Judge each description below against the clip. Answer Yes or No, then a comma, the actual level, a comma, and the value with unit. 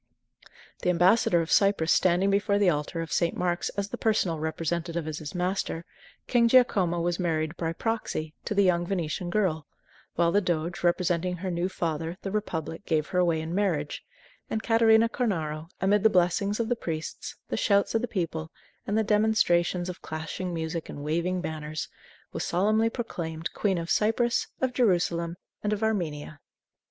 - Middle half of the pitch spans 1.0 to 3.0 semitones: No, average, 3.9 semitones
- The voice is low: No, medium, 175 Hz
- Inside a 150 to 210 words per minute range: Yes, average, 170 wpm